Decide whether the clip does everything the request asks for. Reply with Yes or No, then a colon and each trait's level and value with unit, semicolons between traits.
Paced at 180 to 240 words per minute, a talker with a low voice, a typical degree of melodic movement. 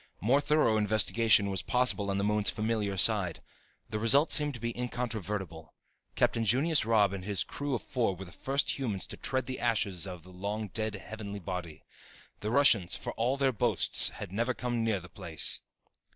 Yes: average, 185 wpm; low, 110 Hz; average, 3.9 semitones